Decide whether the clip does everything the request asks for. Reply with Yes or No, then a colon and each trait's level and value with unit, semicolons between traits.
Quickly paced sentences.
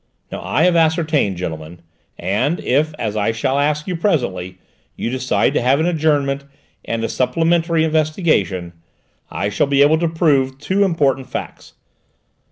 No: average, 155 wpm